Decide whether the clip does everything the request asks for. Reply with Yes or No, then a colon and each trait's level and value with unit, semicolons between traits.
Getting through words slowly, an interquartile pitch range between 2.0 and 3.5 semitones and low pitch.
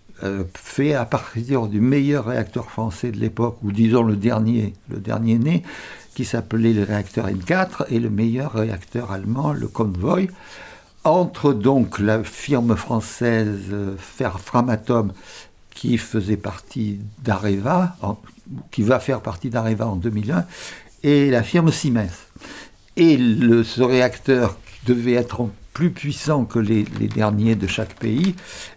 Yes: slow, 135 wpm; average, 3.2 semitones; low, 115 Hz